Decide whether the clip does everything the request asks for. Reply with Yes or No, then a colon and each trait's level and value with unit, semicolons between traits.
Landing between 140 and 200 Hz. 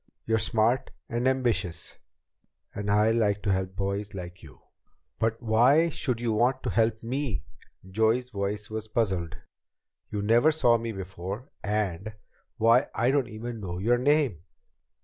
No: low, 110 Hz